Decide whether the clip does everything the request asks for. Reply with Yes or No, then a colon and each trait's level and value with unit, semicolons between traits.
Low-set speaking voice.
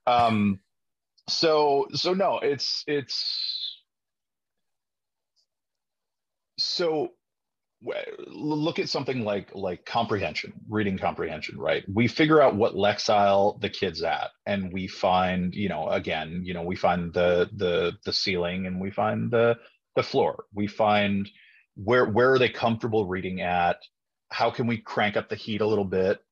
Yes: low, 105 Hz